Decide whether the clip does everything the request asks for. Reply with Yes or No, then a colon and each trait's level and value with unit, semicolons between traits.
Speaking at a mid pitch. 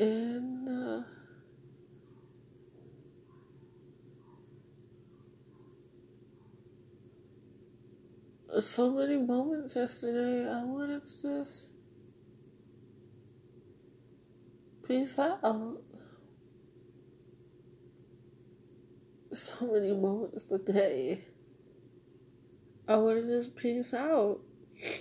No: high, 215 Hz